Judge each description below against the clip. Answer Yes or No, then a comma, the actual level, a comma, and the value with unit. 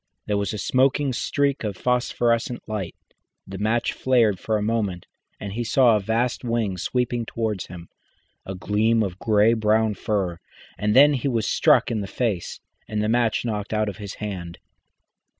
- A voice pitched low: Yes, low, 110 Hz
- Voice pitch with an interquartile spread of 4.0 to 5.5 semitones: No, average, 2.7 semitones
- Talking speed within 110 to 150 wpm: No, average, 175 wpm